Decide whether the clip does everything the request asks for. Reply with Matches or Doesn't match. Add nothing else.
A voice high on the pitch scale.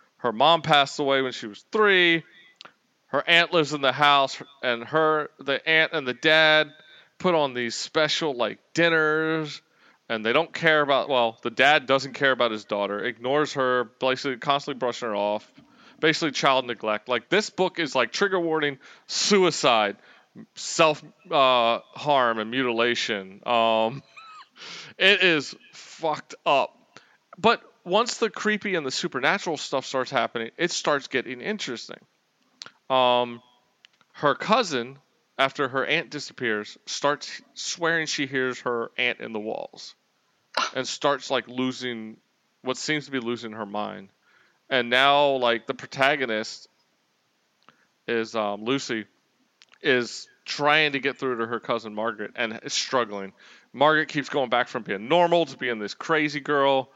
Doesn't match